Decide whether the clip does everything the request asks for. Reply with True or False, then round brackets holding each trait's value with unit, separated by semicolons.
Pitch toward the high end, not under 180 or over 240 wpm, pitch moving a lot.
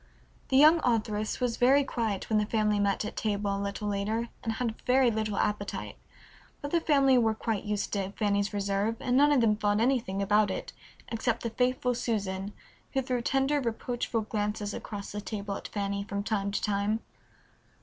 False (215 Hz; 185 wpm; 3.2 semitones)